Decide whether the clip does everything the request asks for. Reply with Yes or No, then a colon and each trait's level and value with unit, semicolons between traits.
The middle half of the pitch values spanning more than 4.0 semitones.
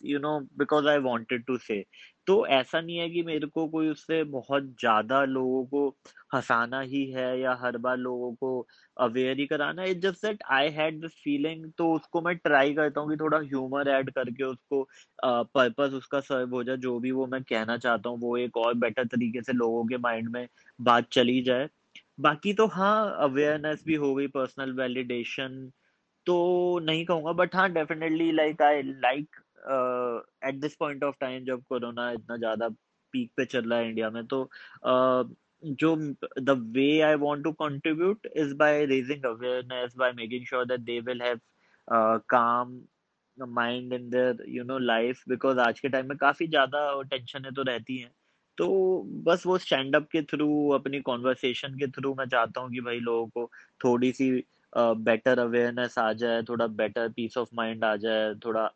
No: average, 3.5 semitones